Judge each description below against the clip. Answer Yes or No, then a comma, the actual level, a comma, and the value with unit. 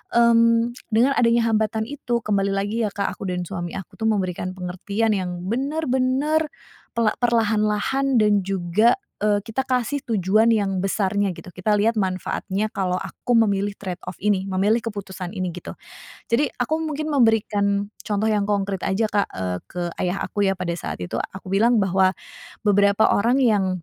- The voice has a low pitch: No, high, 205 Hz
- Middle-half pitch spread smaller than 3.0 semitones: No, average, 3.3 semitones